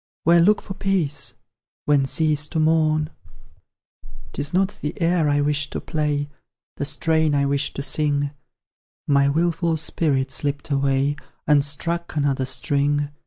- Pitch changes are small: Yes, narrow, 2.2 semitones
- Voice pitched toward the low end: No, medium, 150 Hz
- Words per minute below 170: Yes, average, 140 wpm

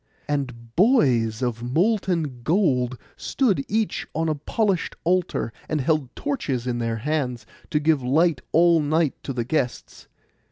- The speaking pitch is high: No, medium, 145 Hz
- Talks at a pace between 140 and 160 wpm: Yes, average, 145 wpm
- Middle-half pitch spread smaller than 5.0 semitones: No, wide, 5.5 semitones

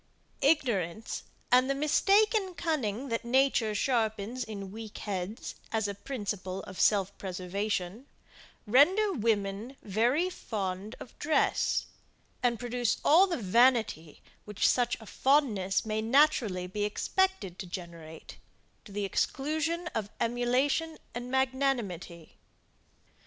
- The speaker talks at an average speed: No, slow, 115 wpm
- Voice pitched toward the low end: No, high, 230 Hz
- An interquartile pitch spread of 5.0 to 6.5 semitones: Yes, wide, 5.4 semitones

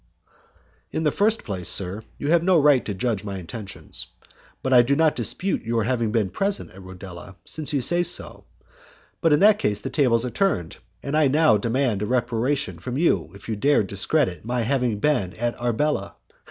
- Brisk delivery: No, average, 195 wpm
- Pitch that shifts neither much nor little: No, wide, 6.4 semitones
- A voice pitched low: Yes, low, 120 Hz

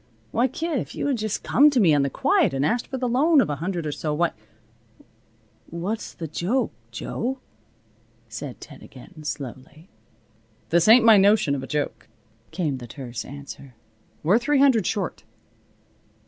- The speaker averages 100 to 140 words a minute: No, average, 175 wpm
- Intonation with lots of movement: Yes, wide, 8.9 semitones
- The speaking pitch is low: No, medium, 170 Hz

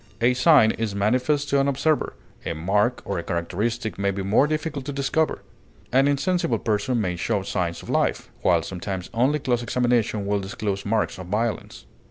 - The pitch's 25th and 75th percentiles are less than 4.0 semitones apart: No, wide, 5.5 semitones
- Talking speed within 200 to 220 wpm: No, average, 180 wpm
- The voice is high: No, low, 115 Hz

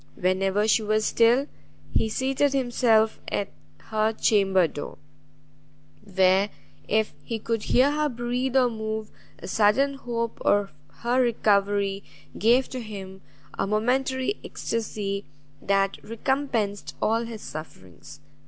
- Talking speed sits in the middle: No, slow, 120 wpm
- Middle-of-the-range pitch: No, high, 220 Hz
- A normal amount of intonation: Yes, average, 3.5 semitones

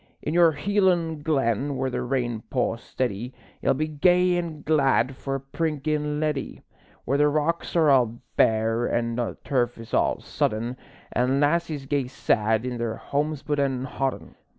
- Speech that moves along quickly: No, average, 160 wpm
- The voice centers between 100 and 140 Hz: Yes, low, 135 Hz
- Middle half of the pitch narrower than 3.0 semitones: No, average, 4.0 semitones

